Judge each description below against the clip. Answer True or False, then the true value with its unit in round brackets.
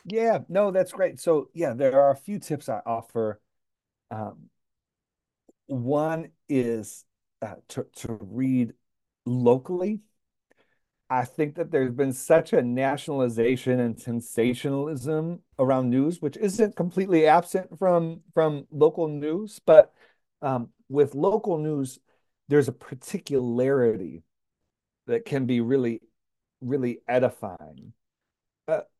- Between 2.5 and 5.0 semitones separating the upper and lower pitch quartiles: False (5.6 semitones)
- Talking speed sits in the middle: False (115 wpm)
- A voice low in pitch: False (145 Hz)